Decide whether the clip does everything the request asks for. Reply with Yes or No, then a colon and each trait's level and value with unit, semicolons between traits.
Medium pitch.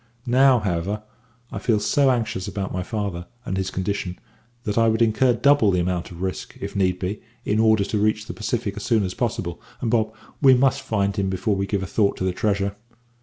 No: low, 105 Hz